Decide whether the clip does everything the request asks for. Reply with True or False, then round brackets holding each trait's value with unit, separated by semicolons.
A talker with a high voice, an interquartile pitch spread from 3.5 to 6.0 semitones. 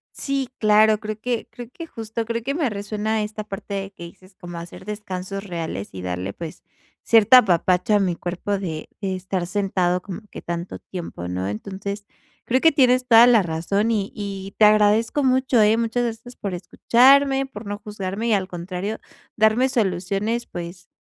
True (205 Hz; 4.0 semitones)